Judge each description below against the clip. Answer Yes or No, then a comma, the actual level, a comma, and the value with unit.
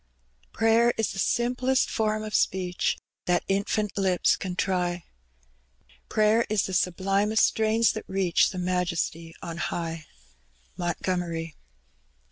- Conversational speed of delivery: No, slow, 110 wpm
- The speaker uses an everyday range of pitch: Yes, average, 3.5 semitones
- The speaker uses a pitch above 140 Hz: Yes, high, 190 Hz